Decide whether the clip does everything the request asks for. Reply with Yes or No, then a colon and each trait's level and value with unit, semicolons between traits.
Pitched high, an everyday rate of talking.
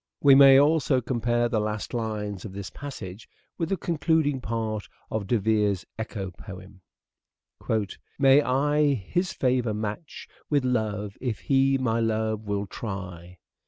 No: low, 115 Hz; average, 145 wpm